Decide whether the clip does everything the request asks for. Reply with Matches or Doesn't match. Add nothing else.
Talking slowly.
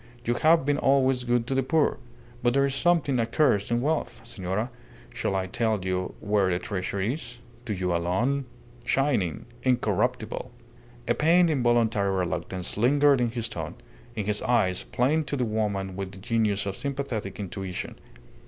Doesn't match